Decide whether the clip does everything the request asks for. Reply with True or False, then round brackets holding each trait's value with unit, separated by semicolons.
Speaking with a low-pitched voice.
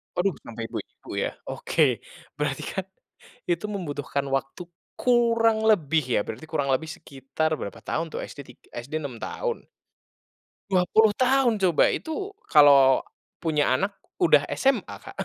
False (165 Hz)